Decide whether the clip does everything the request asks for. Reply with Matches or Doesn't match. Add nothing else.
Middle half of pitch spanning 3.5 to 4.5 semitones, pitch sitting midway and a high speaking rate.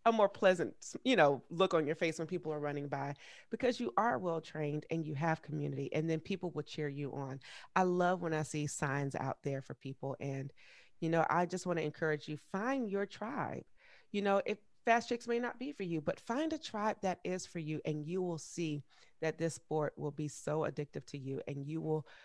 Matches